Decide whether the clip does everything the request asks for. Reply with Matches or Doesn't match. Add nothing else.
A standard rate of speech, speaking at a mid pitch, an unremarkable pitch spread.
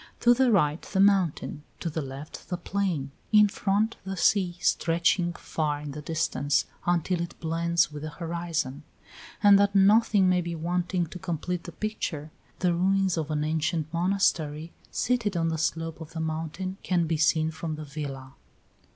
Matches